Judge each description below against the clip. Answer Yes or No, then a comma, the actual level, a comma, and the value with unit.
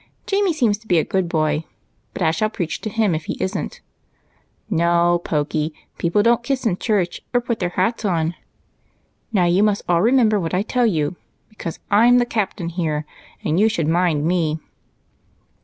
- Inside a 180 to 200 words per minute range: Yes, average, 185 wpm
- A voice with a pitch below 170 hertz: No, medium, 185 Hz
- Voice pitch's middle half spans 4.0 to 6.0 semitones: Yes, average, 4.7 semitones